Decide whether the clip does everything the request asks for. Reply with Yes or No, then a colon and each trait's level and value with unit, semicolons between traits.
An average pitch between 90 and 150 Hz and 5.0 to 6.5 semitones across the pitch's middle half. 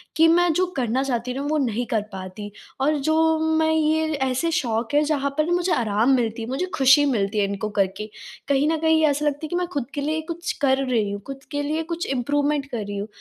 No: very high, 275 Hz; wide, 5.5 semitones